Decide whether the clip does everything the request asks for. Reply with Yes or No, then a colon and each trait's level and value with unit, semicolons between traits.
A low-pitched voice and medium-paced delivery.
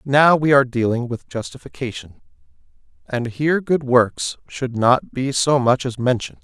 Yes: low, 125 Hz; average, 160 wpm